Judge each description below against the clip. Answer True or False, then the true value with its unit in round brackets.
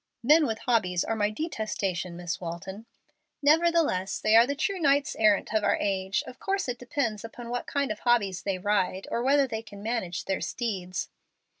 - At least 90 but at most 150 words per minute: False (185 wpm)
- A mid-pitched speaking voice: False (220 Hz)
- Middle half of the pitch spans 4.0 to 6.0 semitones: True (5.0 semitones)